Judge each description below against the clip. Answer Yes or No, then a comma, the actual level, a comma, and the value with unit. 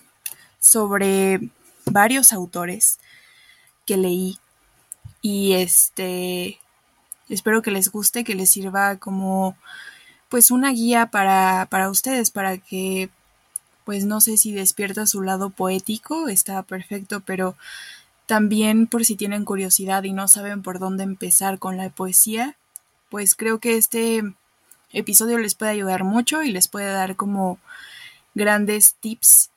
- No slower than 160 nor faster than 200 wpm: No, average, 130 wpm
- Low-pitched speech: No, high, 200 Hz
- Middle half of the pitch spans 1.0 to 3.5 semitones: Yes, narrow, 2.5 semitones